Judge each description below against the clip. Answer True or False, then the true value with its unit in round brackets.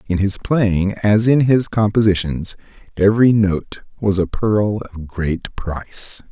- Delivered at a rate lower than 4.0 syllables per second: True (3.8 syllables/s)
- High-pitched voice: False (100 Hz)